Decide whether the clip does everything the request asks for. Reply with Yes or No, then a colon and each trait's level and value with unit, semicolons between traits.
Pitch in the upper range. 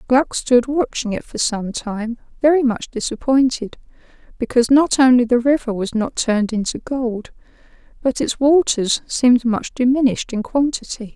Yes: high, 245 Hz